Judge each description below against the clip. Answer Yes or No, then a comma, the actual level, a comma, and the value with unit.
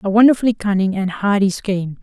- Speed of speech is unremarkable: Yes, average, 180 wpm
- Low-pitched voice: No, high, 205 Hz